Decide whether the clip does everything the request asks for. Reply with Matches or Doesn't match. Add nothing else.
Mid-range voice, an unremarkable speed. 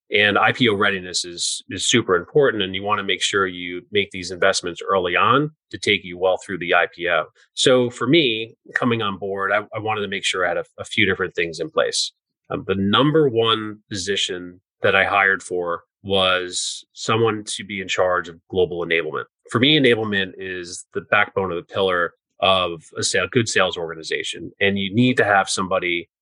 Doesn't match